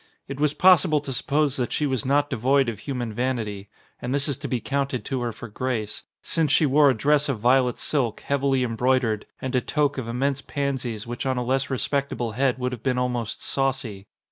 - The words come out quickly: Yes, fast, 210 wpm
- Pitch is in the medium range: No, low, 130 Hz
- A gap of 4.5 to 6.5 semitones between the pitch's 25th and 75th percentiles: No, narrow, 2.5 semitones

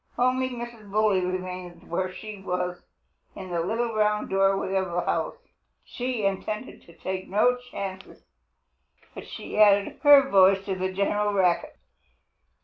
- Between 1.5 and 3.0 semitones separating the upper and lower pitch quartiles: Yes, narrow, 2.5 semitones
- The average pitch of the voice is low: No, high, 195 Hz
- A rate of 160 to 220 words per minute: No, average, 140 wpm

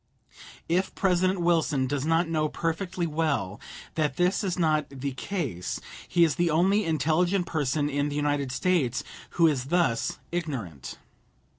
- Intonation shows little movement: No, average, 3.7 semitones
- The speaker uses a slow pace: No, average, 145 wpm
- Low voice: No, medium, 160 Hz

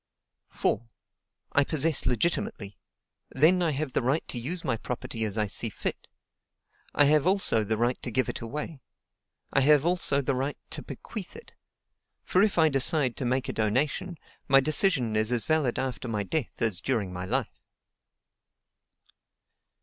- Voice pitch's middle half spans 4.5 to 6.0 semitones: Yes, average, 5.3 semitones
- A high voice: No, low, 135 Hz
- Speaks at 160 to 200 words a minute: Yes, average, 165 wpm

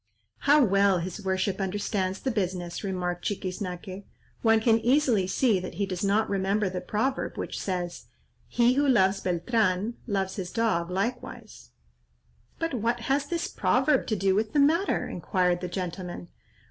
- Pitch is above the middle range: Yes, high, 200 Hz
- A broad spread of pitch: No, average, 4.1 semitones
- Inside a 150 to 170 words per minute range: Yes, average, 155 wpm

